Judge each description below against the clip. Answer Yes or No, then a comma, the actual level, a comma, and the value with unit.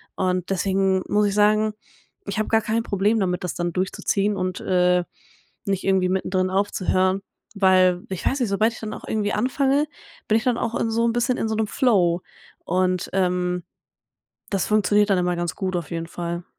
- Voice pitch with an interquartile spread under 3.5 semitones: Yes, average, 2.9 semitones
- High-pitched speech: Yes, high, 195 Hz